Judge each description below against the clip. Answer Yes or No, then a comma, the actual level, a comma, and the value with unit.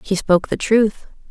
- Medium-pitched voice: No, high, 205 Hz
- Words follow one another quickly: No, average, 185 wpm